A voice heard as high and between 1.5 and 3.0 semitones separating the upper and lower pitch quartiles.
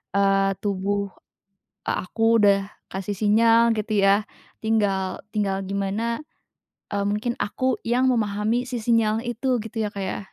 Yes: high, 210 Hz; narrow, 2.5 semitones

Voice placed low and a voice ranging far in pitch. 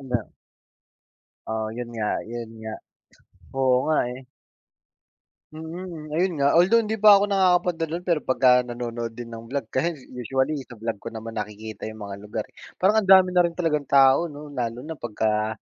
Yes: low, 130 Hz; wide, 6.8 semitones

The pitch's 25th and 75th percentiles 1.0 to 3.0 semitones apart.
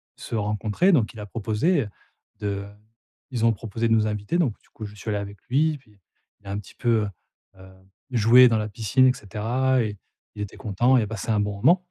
No: average, 3.4 semitones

